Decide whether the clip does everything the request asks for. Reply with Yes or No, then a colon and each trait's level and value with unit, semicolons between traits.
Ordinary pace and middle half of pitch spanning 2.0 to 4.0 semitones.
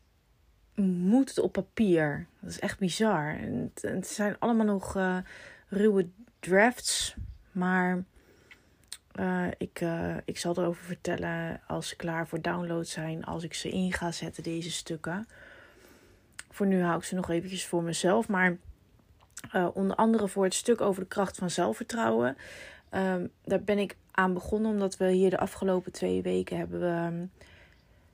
Yes: average, 160 wpm; narrow, 2.6 semitones